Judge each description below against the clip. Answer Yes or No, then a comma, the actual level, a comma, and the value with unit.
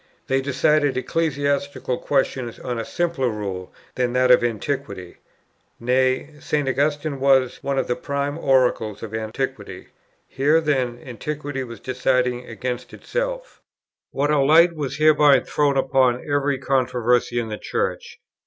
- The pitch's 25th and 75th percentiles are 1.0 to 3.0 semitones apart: Yes, narrow, 2.6 semitones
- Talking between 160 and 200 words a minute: No, slow, 135 wpm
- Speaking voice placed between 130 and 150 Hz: Yes, low, 135 Hz